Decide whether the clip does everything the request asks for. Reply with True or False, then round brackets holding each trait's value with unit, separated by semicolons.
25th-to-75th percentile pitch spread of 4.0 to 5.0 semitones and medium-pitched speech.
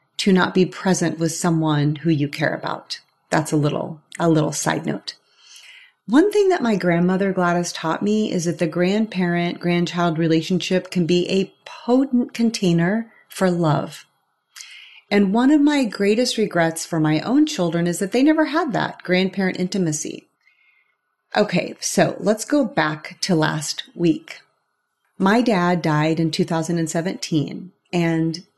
True (4.7 semitones; 180 Hz)